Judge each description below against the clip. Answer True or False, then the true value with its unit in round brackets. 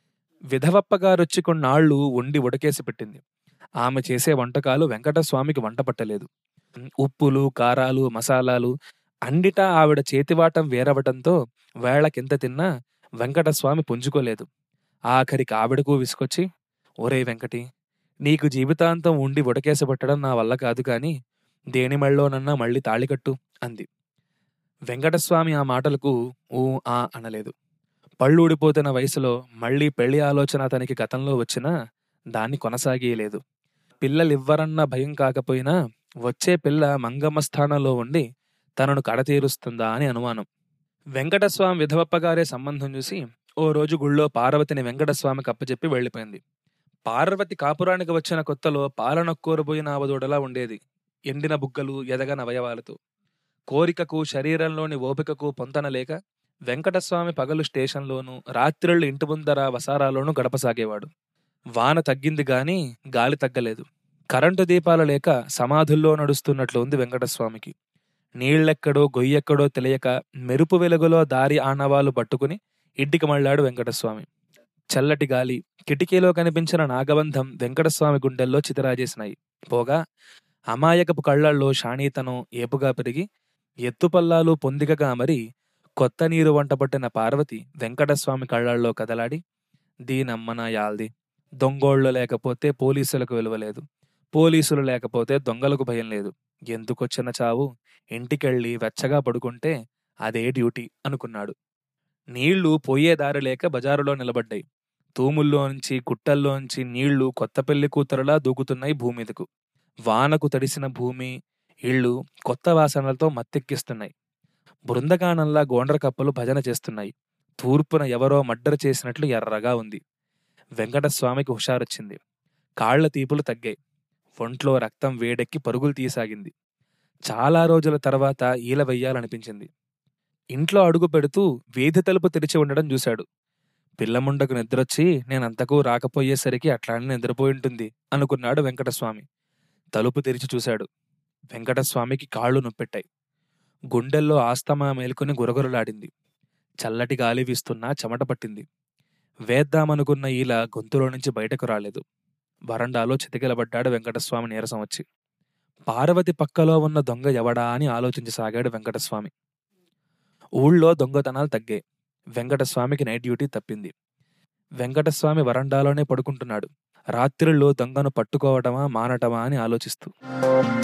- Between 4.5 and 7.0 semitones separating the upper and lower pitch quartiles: False (3.8 semitones)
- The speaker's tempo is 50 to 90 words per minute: False (100 wpm)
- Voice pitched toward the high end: False (140 Hz)